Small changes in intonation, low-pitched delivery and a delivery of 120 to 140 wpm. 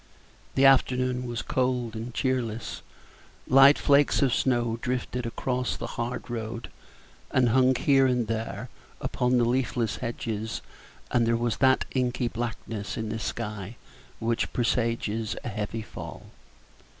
Yes: narrow, 2.0 semitones; low, 120 Hz; slow, 135 wpm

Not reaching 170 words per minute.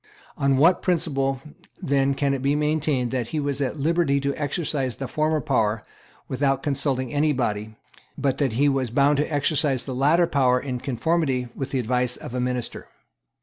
No: average, 180 wpm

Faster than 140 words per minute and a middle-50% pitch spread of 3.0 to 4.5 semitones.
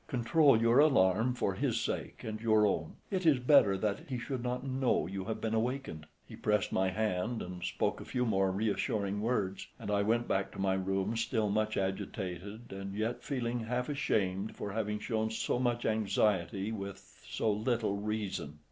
Yes: average, 185 wpm; average, 3.5 semitones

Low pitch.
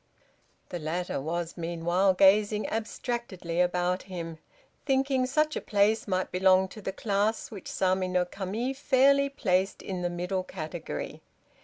No: high, 190 Hz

